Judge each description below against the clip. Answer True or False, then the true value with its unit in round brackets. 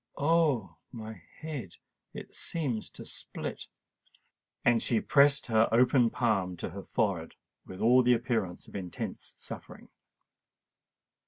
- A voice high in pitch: False (115 Hz)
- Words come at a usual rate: False (115 wpm)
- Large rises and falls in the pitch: False (4.5 semitones)